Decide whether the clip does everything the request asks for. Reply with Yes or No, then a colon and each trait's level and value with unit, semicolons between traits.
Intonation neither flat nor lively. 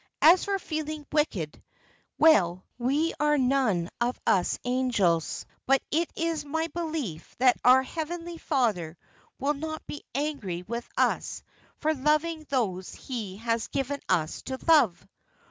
No: wide, 6.6 semitones